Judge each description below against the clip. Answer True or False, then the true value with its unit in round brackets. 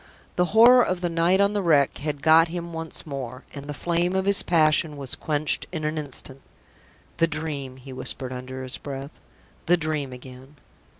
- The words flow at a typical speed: True (185 wpm)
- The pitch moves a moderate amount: True (3.9 semitones)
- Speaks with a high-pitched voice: False (155 Hz)